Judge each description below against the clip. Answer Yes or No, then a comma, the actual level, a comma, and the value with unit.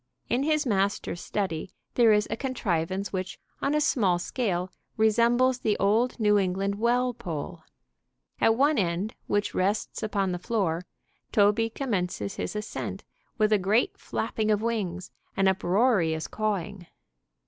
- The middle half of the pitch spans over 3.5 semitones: Yes, average, 3.9 semitones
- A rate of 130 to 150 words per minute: Yes, average, 140 wpm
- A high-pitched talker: Yes, high, 205 Hz